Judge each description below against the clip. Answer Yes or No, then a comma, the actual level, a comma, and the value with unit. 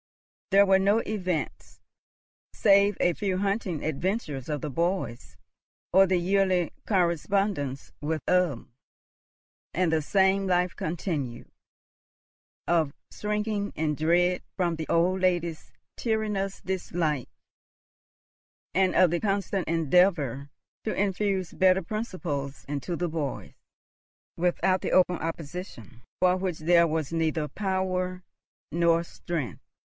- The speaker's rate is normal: No, slow, 115 wpm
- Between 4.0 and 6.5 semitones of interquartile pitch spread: No, average, 3.2 semitones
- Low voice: No, medium, 180 Hz